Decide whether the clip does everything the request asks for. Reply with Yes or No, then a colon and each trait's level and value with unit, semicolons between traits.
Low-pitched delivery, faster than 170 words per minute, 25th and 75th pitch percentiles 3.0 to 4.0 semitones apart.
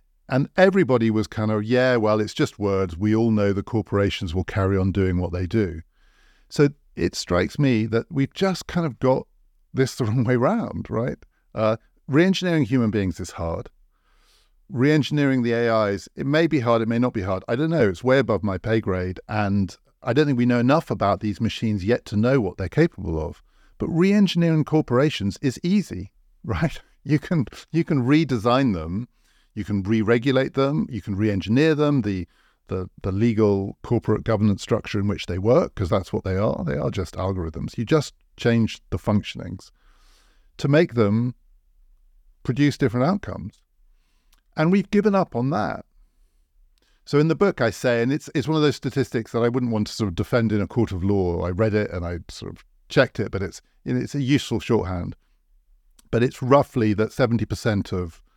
No: low, 110 Hz; average, 190 wpm; wide, 5.6 semitones